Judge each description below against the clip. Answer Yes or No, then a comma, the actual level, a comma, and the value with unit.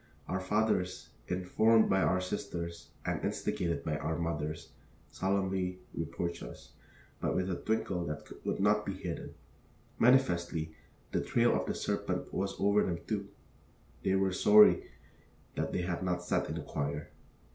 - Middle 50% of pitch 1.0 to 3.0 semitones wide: Yes, average, 2.7 semitones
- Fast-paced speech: No, average, 150 wpm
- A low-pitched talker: Yes, very low, 90 Hz